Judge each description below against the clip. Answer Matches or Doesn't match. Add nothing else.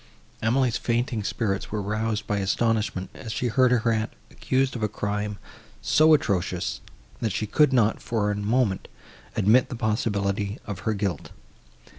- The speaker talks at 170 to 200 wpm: Doesn't match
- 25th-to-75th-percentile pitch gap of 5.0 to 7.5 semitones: Doesn't match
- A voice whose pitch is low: Matches